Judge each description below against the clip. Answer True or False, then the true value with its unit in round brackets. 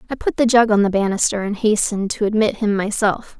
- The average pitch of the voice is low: False (210 Hz)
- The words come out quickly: True (230 wpm)